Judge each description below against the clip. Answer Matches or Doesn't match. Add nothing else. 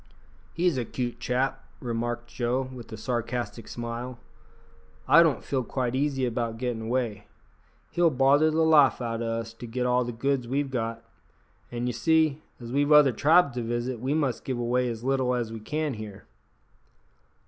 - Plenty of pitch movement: Doesn't match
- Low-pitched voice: Matches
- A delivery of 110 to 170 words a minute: Doesn't match